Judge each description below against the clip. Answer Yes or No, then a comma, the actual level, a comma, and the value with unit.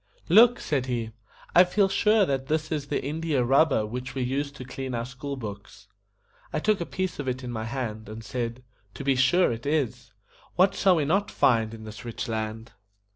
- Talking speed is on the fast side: Yes, fast, 220 wpm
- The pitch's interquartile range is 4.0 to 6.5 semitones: Yes, average, 5.2 semitones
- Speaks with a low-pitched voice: Yes, low, 130 Hz